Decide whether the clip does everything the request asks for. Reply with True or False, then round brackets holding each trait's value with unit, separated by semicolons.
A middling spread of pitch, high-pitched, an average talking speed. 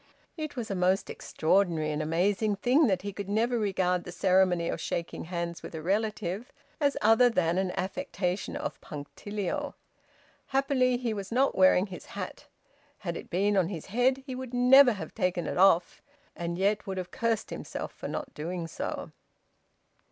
True (4.7 semitones; 195 Hz; 175 wpm)